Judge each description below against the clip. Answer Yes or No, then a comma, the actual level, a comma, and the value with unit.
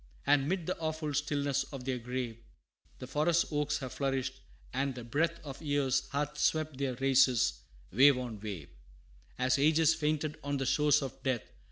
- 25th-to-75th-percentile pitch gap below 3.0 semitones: Yes, narrow, 2.6 semitones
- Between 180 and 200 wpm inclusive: No, average, 170 wpm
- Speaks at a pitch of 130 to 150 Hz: Yes, medium, 140 Hz